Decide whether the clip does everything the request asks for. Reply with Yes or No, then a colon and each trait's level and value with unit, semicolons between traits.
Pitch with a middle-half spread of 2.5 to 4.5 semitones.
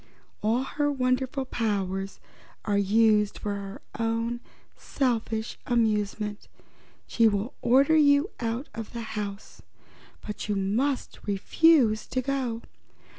Yes: average, 3.7 semitones